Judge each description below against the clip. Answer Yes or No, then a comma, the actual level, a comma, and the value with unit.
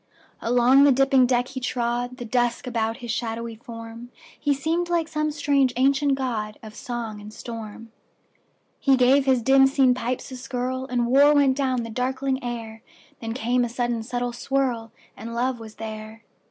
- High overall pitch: Yes, high, 245 Hz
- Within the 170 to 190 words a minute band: No, average, 150 wpm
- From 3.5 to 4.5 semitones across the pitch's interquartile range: No, narrow, 2.6 semitones